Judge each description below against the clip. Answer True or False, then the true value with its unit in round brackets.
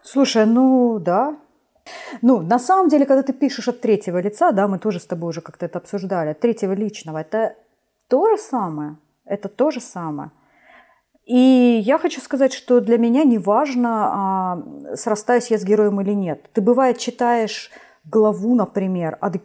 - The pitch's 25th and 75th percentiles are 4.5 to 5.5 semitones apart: True (4.8 semitones)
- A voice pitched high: True (230 Hz)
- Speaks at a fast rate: True (165 wpm)